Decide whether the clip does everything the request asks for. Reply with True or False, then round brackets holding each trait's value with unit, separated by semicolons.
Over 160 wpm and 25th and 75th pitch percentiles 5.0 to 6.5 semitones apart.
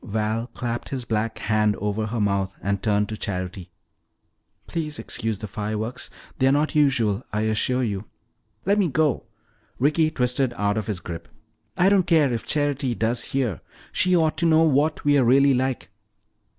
True (170 wpm; 5.3 semitones)